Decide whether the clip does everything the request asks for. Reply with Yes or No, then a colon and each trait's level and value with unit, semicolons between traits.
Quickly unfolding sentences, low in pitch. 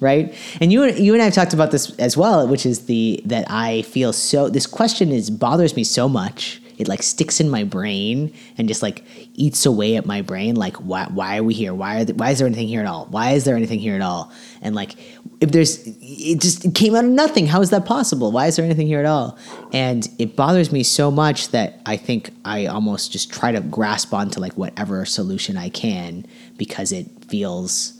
No: fast, 235 wpm; medium, 160 Hz